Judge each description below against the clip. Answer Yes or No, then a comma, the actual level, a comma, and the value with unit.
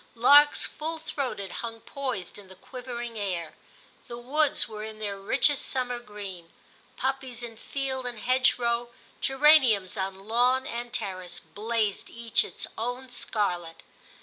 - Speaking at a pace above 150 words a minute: No, slow, 135 wpm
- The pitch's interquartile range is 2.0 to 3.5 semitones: No, average, 4.2 semitones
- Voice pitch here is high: Yes, high, 235 Hz